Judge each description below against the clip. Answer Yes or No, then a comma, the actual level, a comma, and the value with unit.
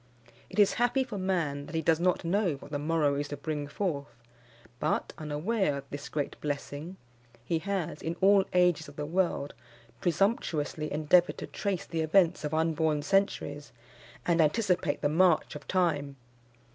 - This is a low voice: No, medium, 160 Hz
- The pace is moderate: Yes, average, 165 wpm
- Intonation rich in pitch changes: No, average, 4.1 semitones